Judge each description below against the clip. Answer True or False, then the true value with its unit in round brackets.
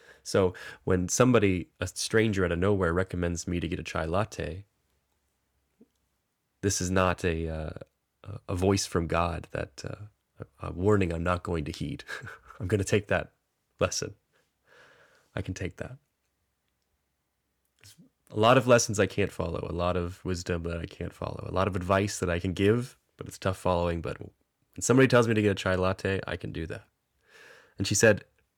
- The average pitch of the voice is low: True (95 Hz)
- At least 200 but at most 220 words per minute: False (185 wpm)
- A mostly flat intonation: False (3.2 semitones)